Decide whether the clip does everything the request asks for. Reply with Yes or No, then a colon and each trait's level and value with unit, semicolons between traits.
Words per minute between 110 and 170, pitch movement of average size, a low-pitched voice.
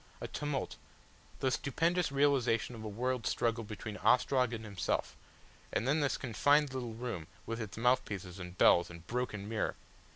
Yes: average, 165 wpm; average, 3.8 semitones; low, 120 Hz